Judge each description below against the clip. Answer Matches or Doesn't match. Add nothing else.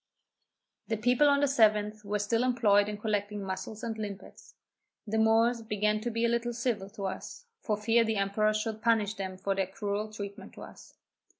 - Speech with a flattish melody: Matches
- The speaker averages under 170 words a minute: Doesn't match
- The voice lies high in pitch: Matches